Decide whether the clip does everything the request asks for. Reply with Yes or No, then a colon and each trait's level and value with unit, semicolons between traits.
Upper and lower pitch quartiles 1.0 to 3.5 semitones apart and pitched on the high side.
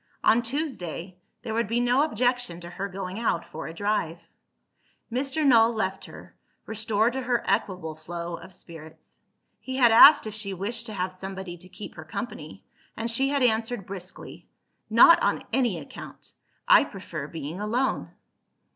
No: average, 4.8 semitones; high, 215 Hz